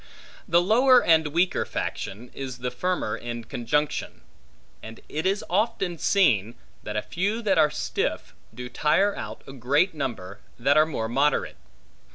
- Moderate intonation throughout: No, wide, 7.1 semitones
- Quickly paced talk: No, average, 155 wpm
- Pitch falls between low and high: Yes, medium, 150 Hz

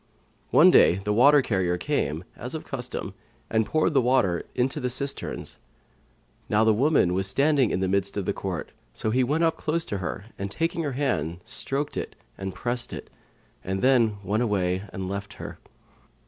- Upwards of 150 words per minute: Yes, average, 180 wpm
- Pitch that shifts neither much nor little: No, wide, 5.8 semitones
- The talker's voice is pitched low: Yes, low, 110 Hz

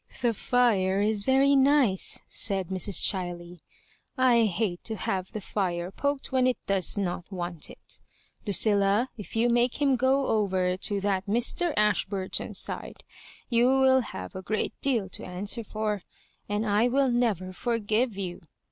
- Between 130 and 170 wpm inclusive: Yes, average, 160 wpm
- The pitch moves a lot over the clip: No, average, 4.4 semitones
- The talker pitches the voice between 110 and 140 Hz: No, high, 210 Hz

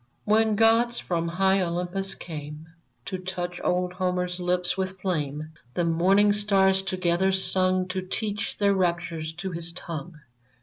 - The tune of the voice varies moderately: No, narrow, 2.0 semitones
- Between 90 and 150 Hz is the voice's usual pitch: No, medium, 185 Hz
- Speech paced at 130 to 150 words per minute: Yes, average, 140 wpm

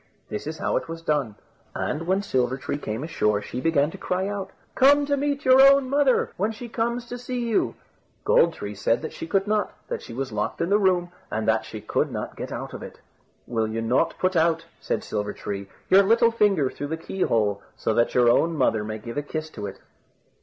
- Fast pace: Yes, fast, 230 wpm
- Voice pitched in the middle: Yes, medium, 160 Hz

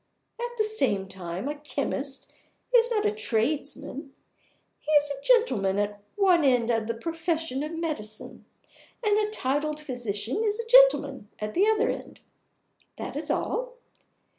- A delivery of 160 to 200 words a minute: No, average, 150 wpm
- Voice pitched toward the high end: Yes, very high, 295 Hz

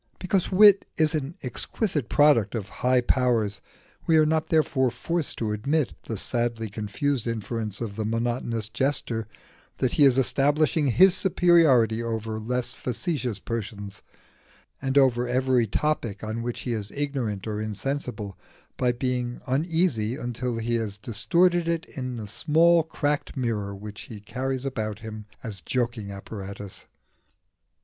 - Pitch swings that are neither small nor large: Yes, average, 4.7 semitones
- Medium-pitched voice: No, low, 120 Hz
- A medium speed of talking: Yes, average, 150 wpm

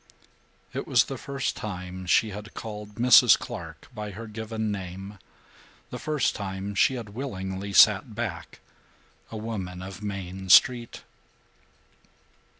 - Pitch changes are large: No, average, 2.8 semitones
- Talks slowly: Yes, slow, 130 wpm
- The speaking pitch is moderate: No, low, 105 Hz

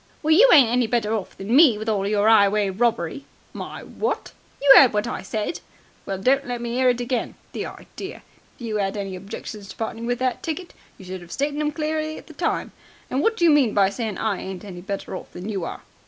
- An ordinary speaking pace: No, fast, 235 wpm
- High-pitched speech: Yes, high, 225 Hz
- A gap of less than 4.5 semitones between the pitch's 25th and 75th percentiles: No, average, 5.2 semitones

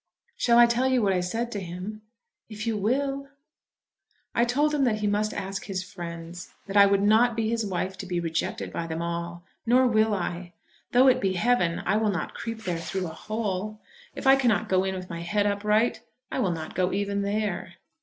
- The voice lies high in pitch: Yes, high, 205 Hz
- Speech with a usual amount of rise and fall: Yes, average, 4.0 semitones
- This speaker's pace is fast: Yes, fast, 215 wpm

